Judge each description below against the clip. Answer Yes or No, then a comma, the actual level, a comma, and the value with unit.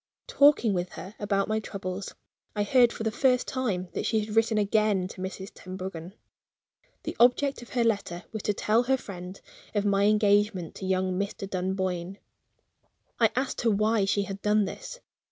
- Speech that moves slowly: No, average, 175 wpm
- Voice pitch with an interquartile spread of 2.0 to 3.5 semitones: Yes, average, 3.0 semitones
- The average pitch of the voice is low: No, high, 205 Hz